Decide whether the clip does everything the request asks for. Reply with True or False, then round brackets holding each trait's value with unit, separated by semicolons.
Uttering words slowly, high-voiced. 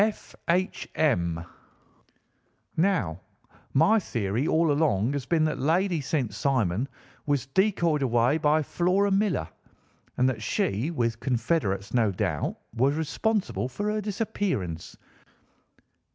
False (120 wpm; 145 Hz)